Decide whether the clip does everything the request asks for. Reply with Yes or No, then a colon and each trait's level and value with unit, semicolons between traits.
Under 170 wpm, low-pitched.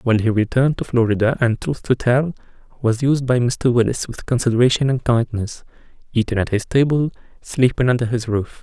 No: average, 180 wpm; low, 120 Hz